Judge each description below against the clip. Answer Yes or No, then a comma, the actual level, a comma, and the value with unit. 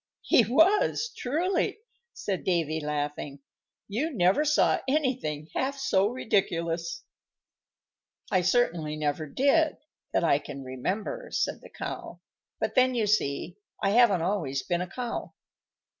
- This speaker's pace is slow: Yes, slow, 130 wpm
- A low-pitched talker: No, high, 195 Hz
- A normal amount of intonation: No, wide, 8.8 semitones